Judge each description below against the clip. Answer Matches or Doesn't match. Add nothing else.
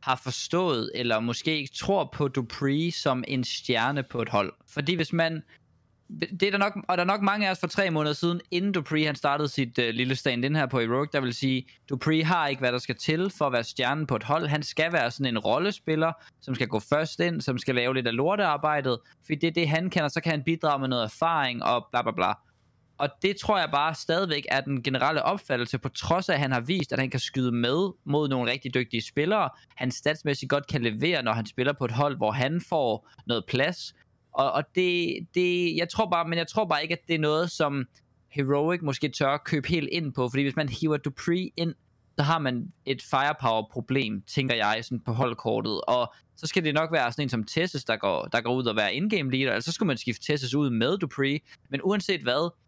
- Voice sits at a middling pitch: Matches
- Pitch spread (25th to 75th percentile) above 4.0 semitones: Matches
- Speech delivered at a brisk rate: Matches